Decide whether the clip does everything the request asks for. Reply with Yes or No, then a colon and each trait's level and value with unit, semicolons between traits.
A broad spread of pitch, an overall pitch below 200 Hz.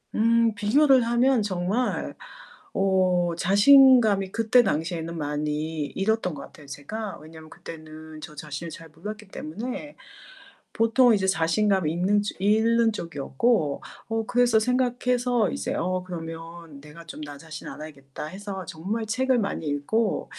Yes: wide, 6.1 semitones; high, 190 Hz